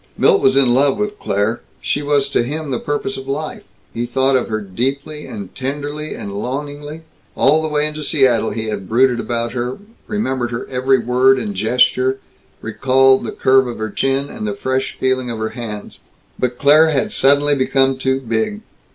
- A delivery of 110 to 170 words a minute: No, average, 185 wpm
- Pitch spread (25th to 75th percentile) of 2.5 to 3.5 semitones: Yes, average, 3.2 semitones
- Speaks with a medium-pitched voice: No, low, 130 Hz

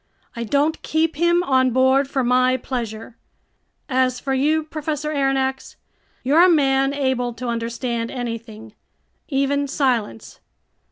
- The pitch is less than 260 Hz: No, very high, 265 Hz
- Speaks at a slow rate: Yes, slow, 125 wpm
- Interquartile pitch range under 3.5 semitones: Yes, average, 2.7 semitones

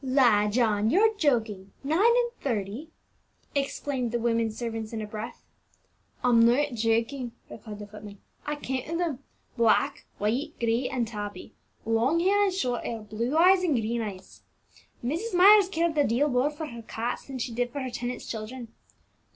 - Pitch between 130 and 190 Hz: No, high, 245 Hz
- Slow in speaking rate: No, average, 165 wpm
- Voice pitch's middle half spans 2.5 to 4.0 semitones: No, average, 4.7 semitones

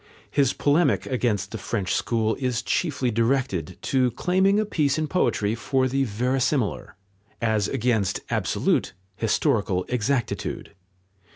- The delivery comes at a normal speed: No, slow, 120 wpm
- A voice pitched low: Yes, low, 125 Hz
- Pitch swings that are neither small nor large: Yes, average, 4.0 semitones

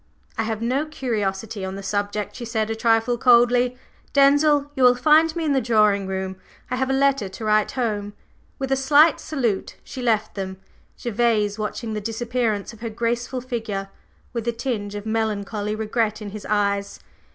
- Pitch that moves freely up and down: No, average, 3.3 semitones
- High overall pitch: Yes, high, 225 Hz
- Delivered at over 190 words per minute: No, average, 180 wpm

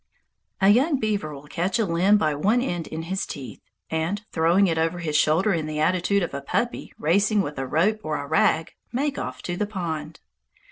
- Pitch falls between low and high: Yes, medium, 170 Hz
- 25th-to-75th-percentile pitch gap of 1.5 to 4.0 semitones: No, average, 4.6 semitones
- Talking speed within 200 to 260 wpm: Yes, fast, 205 wpm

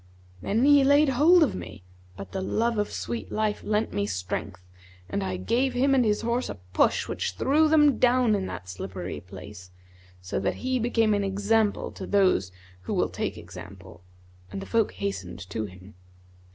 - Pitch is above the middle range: Yes, high, 200 Hz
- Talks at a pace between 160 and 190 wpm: Yes, average, 180 wpm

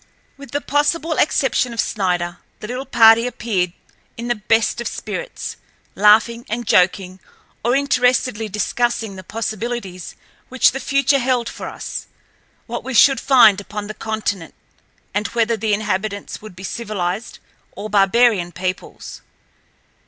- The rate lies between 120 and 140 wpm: Yes, slow, 135 wpm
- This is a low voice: No, high, 225 Hz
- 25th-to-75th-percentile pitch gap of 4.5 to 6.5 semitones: No, average, 3.4 semitones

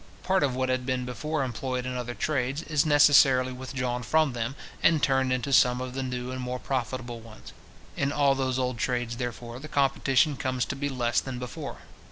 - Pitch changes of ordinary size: No, narrow, 1.7 semitones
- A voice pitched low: Yes, low, 130 Hz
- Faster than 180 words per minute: Yes, average, 200 wpm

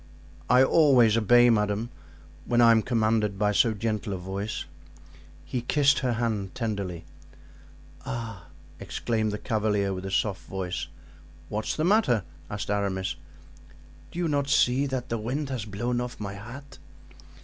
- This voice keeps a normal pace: Yes, average, 150 wpm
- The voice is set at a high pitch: No, low, 110 Hz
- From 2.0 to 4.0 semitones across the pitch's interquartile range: Yes, average, 3.4 semitones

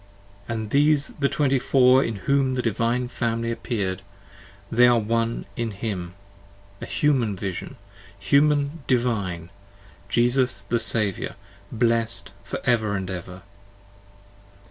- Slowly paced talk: Yes, slow, 125 wpm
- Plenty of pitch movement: No, average, 4.0 semitones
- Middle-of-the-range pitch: No, low, 115 Hz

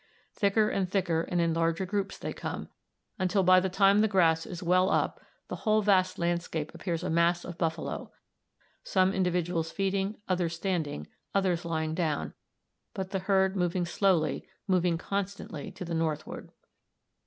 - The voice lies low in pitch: No, medium, 180 Hz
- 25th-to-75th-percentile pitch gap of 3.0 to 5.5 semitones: No, narrow, 2.5 semitones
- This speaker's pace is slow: No, average, 155 wpm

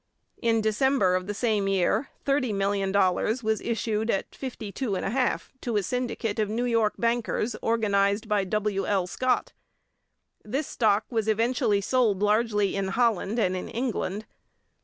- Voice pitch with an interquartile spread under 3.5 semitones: Yes, average, 2.9 semitones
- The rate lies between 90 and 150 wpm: Yes, average, 140 wpm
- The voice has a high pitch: Yes, high, 215 Hz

